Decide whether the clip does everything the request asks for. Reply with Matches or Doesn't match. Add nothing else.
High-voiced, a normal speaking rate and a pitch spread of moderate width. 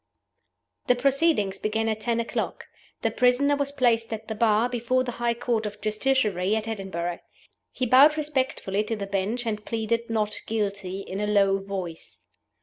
Matches